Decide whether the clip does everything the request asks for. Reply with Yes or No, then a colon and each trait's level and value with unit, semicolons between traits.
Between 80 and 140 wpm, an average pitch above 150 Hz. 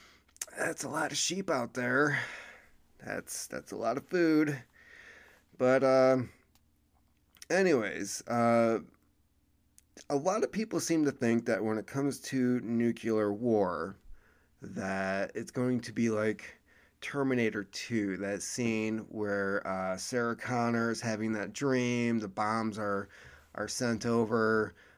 No: slow, 135 wpm; low, 115 Hz